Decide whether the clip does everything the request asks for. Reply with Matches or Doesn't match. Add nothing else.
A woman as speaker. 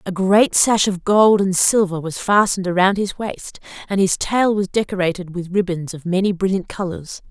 Matches